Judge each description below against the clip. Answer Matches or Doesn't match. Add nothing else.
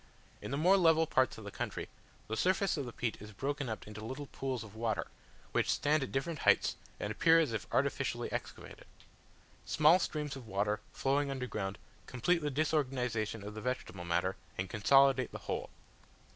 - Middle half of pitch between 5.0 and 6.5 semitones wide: Matches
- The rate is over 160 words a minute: Matches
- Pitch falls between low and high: Doesn't match